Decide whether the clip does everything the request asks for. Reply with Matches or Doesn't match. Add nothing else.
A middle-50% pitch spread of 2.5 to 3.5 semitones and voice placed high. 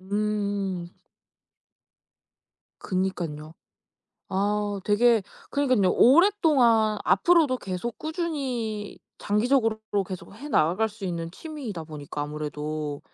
Doesn't match